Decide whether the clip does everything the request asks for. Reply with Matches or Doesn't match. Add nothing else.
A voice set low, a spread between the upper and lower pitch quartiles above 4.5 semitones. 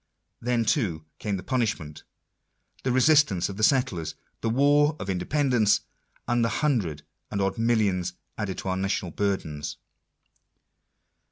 Matches